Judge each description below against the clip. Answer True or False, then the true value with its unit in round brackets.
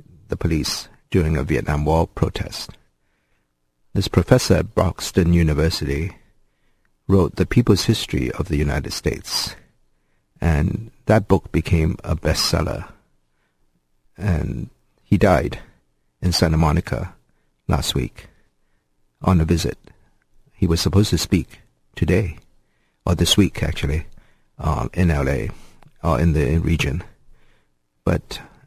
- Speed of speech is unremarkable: False (120 wpm)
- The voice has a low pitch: True (80 Hz)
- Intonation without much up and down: False (4.2 semitones)